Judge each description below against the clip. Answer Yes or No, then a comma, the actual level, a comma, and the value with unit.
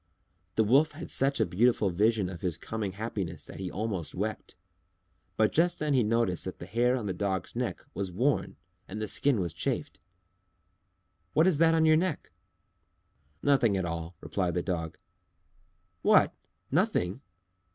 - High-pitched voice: No, low, 110 Hz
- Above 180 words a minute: No, average, 160 wpm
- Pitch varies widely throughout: Yes, wide, 6.3 semitones